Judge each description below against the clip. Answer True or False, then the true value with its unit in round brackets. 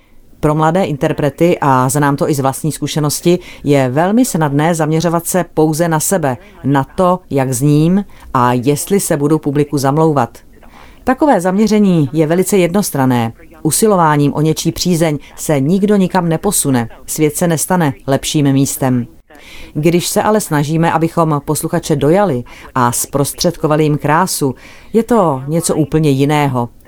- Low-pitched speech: False (155 Hz)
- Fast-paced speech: False (140 wpm)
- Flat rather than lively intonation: False (3.6 semitones)